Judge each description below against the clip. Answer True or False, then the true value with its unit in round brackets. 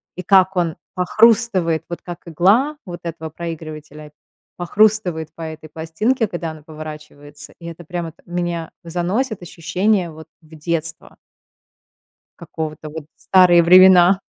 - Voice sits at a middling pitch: True (170 Hz)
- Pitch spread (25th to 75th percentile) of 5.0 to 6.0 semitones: False (2.7 semitones)